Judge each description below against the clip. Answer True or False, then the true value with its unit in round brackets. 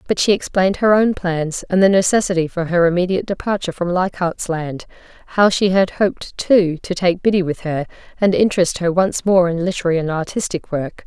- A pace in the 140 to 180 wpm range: False (190 wpm)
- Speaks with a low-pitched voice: False (180 Hz)